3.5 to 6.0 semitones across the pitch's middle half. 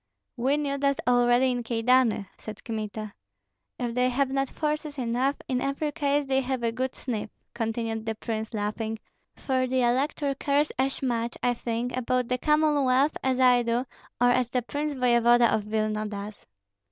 No: average, 2.8 semitones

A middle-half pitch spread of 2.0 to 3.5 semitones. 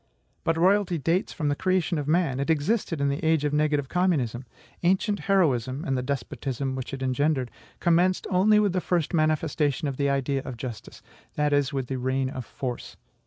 No: average, 4.4 semitones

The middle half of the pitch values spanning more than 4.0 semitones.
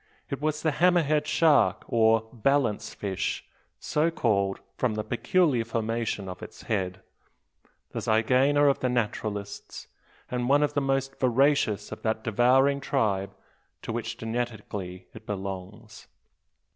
Yes: average, 4.6 semitones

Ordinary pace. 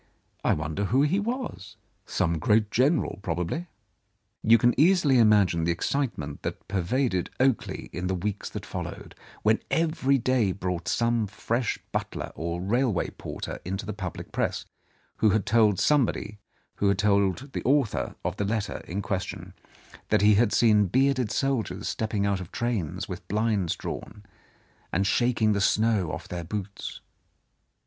Yes: average, 155 wpm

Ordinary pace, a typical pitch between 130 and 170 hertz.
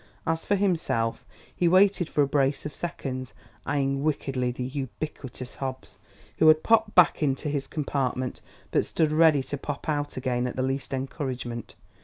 Yes: average, 165 wpm; medium, 140 Hz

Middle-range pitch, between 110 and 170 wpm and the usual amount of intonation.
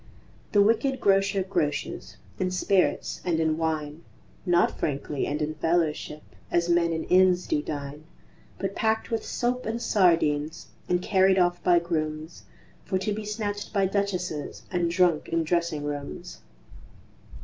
Yes: medium, 175 Hz; average, 145 wpm; average, 4.0 semitones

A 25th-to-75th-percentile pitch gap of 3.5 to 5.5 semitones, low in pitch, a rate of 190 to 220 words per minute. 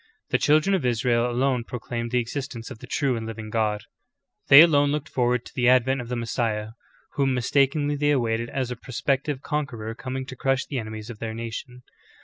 No: average, 2.9 semitones; low, 125 Hz; average, 195 wpm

